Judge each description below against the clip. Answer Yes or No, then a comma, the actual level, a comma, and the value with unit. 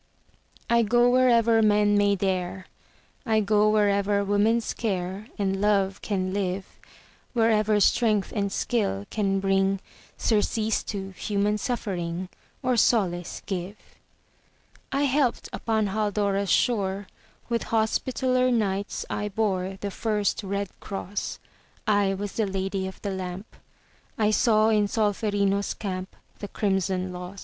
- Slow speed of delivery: Yes, slow, 125 wpm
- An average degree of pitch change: No, narrow, 2.2 semitones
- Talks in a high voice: Yes, high, 205 Hz